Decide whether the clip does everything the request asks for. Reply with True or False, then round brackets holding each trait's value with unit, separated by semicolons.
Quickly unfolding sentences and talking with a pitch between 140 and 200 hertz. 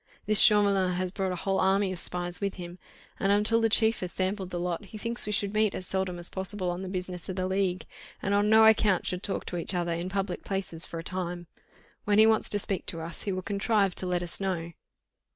True (245 wpm; 190 Hz)